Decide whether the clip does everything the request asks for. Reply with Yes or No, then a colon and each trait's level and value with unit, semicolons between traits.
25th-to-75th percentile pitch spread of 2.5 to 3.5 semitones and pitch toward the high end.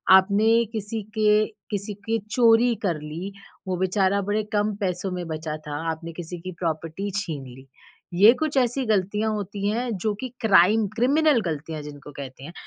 No: average, 4.8 semitones; high, 200 Hz